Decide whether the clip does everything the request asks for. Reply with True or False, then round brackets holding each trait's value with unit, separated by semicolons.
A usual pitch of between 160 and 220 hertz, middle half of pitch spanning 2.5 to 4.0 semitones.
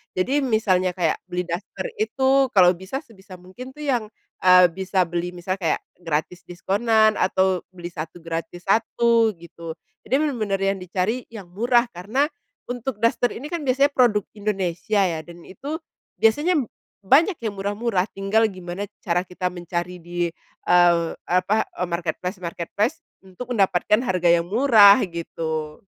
False (190 Hz; 4.7 semitones)